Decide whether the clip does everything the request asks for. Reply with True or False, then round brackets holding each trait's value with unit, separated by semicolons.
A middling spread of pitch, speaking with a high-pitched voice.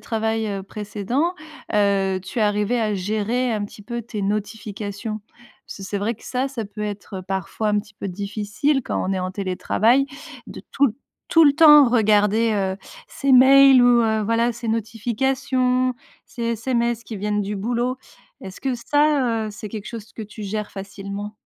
True (3.1 semitones; 220 Hz)